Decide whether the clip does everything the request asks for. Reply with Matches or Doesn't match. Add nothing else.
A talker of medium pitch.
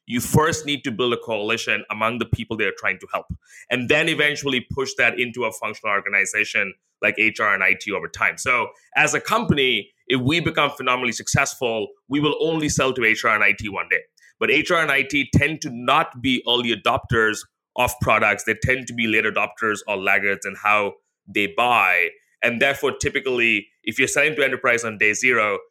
Doesn't match